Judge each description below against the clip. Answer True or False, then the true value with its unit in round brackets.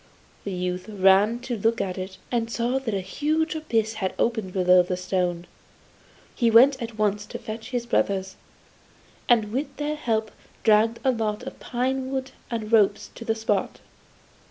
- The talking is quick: False (170 wpm)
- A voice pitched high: True (220 Hz)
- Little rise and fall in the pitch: False (3.8 semitones)